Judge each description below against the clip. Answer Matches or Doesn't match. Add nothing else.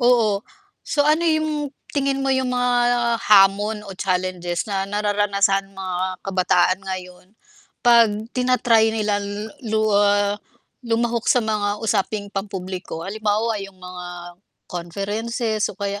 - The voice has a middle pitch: Doesn't match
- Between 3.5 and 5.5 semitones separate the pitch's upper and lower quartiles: Doesn't match